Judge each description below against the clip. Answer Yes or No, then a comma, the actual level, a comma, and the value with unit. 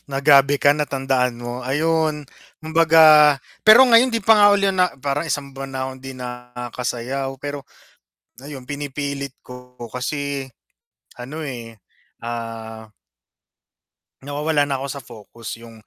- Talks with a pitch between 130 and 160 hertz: Yes, medium, 140 Hz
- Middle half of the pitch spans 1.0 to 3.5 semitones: Yes, average, 3.2 semitones